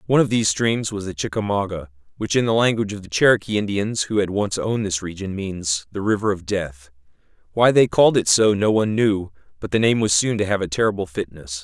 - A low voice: Yes, low, 100 Hz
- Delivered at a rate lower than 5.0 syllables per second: No, 6.1 syllables/s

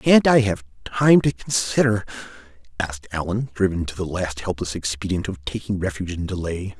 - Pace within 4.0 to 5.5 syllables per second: Yes, 5.4 syllables/s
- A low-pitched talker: Yes, very low, 95 Hz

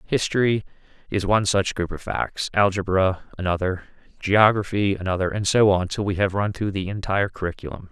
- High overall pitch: No, low, 100 Hz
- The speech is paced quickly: No, average, 165 wpm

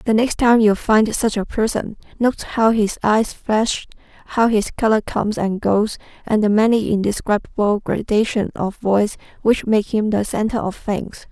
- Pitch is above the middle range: Yes, high, 215 Hz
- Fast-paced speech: No, average, 175 wpm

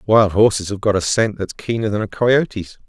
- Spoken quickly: Yes, fast, 230 wpm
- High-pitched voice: No, low, 105 Hz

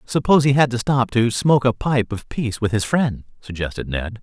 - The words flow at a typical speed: No, fast, 225 wpm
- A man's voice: Yes, male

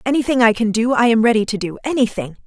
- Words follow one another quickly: Yes, fast, 245 wpm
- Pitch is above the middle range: Yes, high, 230 Hz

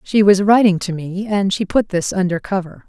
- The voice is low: No, high, 190 Hz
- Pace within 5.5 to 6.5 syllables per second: No, 5.1 syllables/s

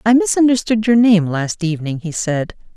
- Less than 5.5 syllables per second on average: Yes, 5.2 syllables/s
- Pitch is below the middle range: No, high, 200 Hz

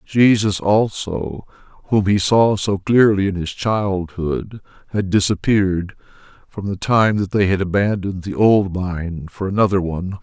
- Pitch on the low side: Yes, very low, 95 Hz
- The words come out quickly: No, average, 145 wpm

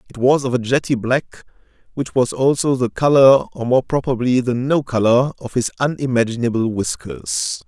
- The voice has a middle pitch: No, low, 125 Hz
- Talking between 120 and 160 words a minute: Yes, average, 155 wpm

